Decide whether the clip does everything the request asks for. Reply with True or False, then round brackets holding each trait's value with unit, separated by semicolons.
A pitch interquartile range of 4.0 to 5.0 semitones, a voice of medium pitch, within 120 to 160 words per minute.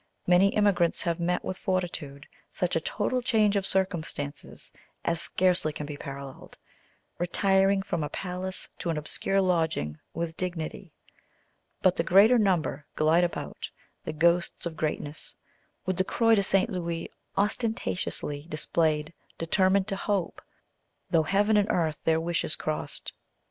False (3.4 semitones; 175 Hz; 140 wpm)